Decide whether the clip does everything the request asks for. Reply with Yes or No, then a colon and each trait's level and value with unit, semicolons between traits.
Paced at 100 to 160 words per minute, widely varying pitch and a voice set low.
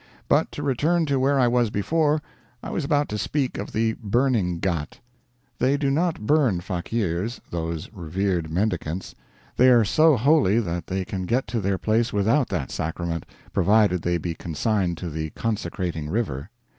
No: average, 170 wpm; wide, 6.8 semitones; low, 105 Hz